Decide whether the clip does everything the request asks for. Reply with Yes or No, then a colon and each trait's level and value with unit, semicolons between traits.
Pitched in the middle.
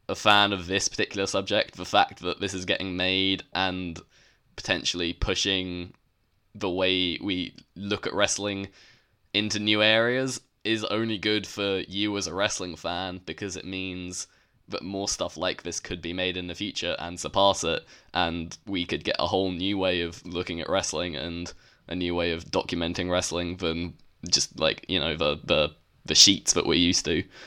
No: very low, 95 Hz